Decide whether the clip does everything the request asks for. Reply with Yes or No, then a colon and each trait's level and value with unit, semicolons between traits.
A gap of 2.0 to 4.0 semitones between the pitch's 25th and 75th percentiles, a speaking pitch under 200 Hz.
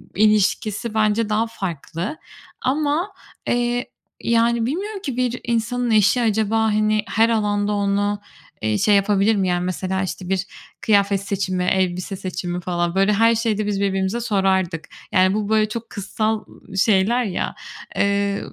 No: average, 2.9 semitones; high, 210 Hz